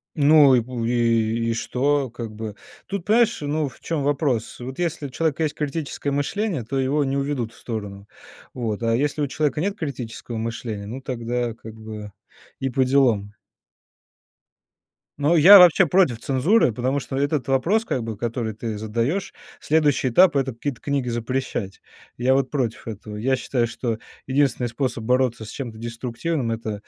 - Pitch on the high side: No, low, 130 Hz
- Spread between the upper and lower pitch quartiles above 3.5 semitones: Yes, average, 4.1 semitones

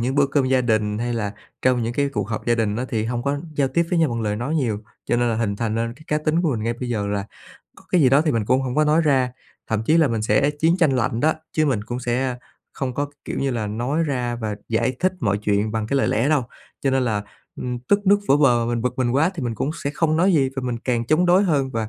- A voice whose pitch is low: Yes, low, 125 Hz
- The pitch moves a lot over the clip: No, average, 4.1 semitones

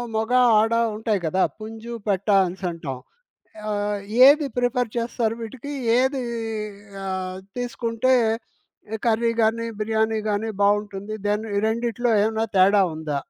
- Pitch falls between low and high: No, high, 220 Hz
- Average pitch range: No, narrow, 2.3 semitones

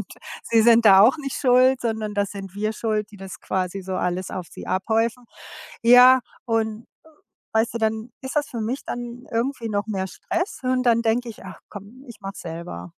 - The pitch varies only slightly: No, average, 3.8 semitones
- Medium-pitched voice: No, high, 225 Hz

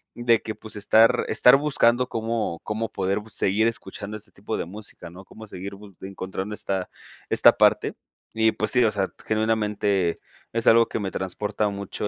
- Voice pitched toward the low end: Yes, low, 105 Hz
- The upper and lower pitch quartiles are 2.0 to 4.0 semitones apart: Yes, narrow, 2.4 semitones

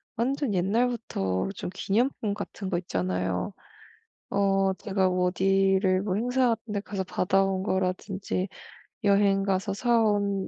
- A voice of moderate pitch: No, high, 195 Hz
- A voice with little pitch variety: Yes, narrow, 2.1 semitones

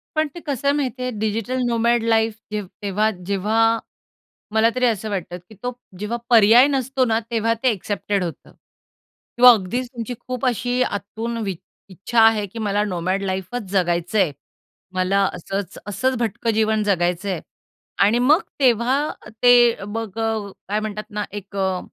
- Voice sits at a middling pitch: No, high, 220 Hz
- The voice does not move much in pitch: No, average, 3.3 semitones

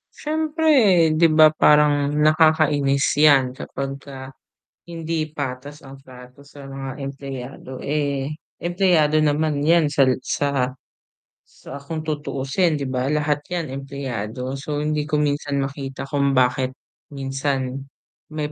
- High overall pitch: No, medium, 140 Hz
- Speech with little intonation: Yes, narrow, 2.2 semitones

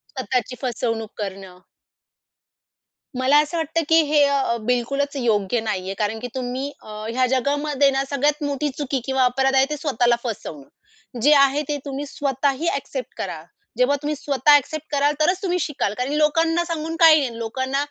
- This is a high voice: Yes, very high, 275 Hz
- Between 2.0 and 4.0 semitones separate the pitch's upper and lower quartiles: Yes, average, 3.4 semitones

